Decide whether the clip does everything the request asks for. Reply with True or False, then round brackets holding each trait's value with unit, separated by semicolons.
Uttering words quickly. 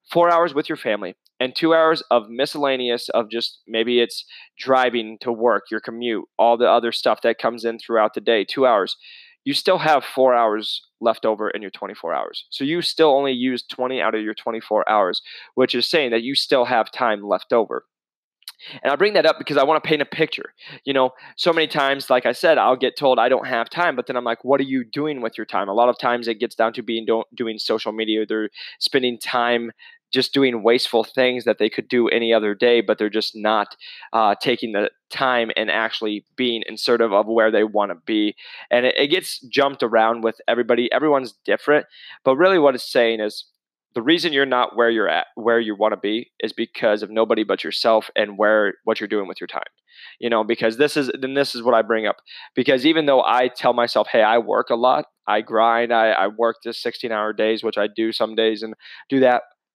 True (230 wpm)